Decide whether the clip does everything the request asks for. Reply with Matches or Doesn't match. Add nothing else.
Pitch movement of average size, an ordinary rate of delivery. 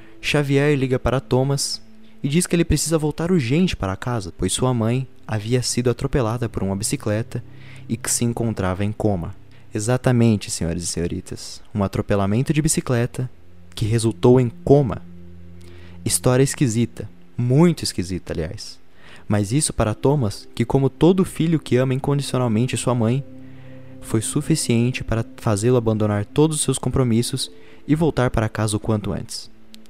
Matches